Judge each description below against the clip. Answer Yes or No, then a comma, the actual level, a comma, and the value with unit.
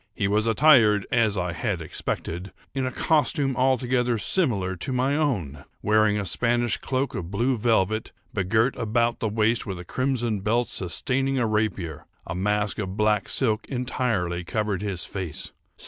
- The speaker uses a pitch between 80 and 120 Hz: Yes, low, 110 Hz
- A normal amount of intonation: Yes, average, 4.3 semitones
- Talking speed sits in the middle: Yes, average, 160 wpm